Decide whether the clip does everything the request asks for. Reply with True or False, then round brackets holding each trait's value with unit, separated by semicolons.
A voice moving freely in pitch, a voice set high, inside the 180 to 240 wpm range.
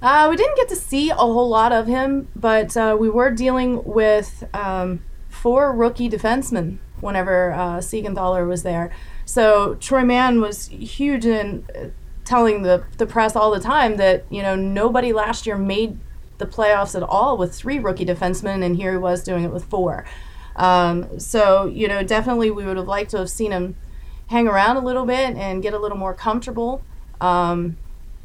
False (4.4 semitones; 210 Hz; 185 wpm)